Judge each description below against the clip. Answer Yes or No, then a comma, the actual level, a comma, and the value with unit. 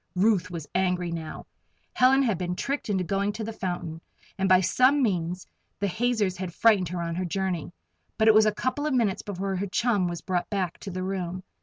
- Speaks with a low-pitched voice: No, high, 190 Hz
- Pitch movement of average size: Yes, average, 3.3 semitones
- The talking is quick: Yes, fast, 210 wpm